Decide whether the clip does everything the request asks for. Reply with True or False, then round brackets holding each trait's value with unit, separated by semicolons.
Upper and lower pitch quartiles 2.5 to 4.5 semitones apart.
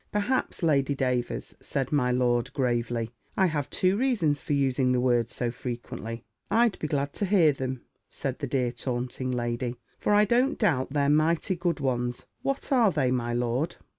False (5.3 semitones)